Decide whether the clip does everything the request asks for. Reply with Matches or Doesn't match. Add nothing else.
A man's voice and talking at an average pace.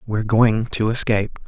Matches